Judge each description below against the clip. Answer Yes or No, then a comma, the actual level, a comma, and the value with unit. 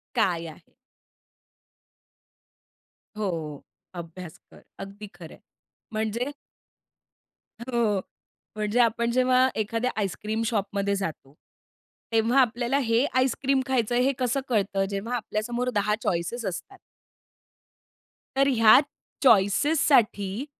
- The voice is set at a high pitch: Yes, high, 220 Hz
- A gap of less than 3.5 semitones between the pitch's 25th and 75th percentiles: No, average, 3.8 semitones